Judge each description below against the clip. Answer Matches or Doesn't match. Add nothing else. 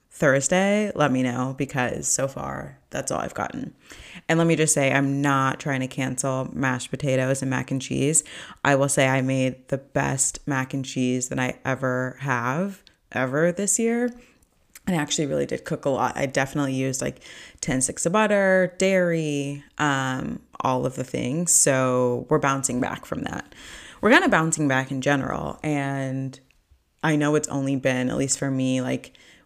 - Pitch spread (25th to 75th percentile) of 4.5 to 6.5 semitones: Doesn't match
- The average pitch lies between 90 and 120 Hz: Doesn't match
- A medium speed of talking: Matches